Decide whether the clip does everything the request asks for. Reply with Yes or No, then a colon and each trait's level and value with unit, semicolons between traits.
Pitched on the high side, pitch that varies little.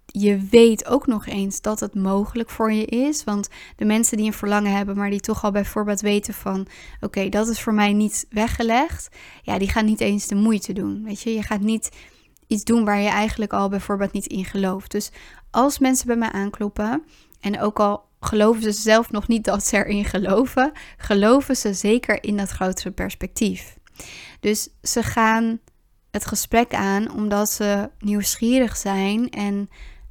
Yes: high, 210 Hz; narrow, 2.0 semitones